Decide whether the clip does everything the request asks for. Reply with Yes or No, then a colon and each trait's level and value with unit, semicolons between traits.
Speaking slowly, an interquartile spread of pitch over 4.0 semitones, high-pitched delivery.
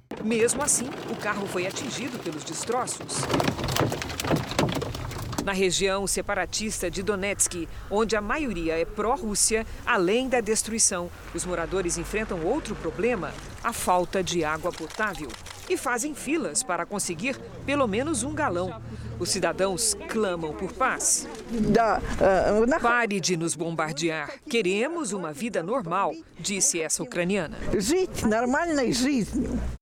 Yes: slow, 115 wpm; average, 5.2 semitones; high, 205 Hz